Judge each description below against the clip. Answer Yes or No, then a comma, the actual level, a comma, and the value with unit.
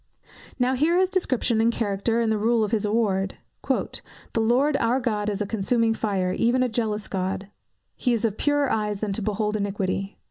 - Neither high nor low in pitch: No, high, 220 Hz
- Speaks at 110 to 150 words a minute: No, average, 190 wpm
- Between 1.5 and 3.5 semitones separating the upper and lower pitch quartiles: Yes, average, 2.8 semitones